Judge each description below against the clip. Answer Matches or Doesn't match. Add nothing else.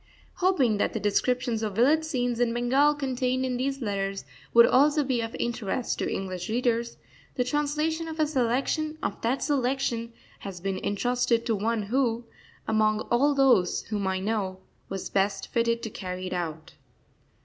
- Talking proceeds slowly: Doesn't match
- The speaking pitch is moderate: Doesn't match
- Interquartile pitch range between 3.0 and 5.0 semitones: Matches